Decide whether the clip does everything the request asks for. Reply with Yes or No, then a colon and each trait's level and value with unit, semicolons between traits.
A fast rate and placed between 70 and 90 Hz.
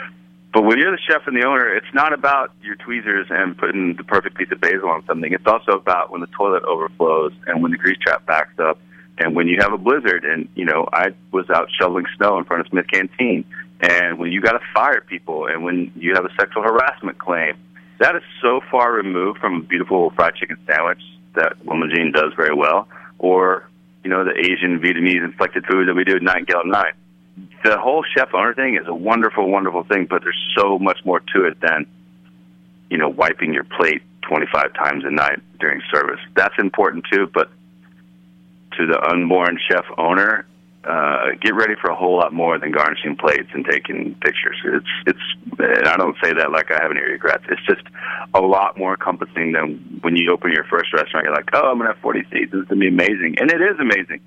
Yes: fast, 220 wpm; very low, 85 Hz